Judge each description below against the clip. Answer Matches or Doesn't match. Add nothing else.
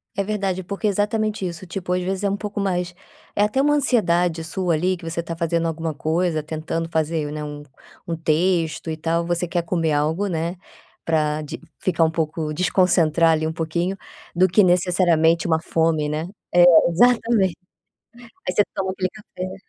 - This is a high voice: Doesn't match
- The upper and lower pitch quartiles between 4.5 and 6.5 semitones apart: Doesn't match